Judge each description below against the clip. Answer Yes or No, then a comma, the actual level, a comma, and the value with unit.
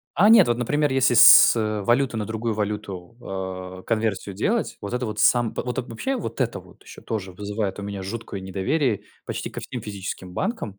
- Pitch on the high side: No, low, 110 Hz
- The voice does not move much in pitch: No, average, 3.6 semitones